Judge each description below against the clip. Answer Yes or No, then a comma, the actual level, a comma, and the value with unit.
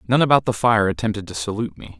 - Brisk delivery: Yes, fast, 240 wpm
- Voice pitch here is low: Yes, low, 105 Hz